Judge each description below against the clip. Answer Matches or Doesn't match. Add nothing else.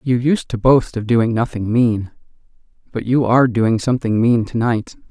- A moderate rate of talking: Matches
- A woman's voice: Doesn't match